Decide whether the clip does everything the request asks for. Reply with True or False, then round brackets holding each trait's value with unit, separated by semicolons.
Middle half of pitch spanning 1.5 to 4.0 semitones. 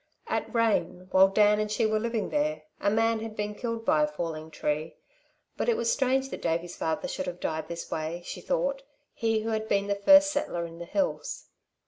False (5.3 semitones)